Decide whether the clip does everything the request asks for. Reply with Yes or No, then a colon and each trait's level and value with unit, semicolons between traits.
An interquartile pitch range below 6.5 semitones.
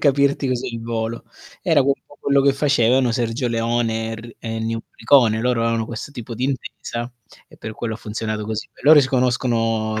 Yes: average, 2.7 semitones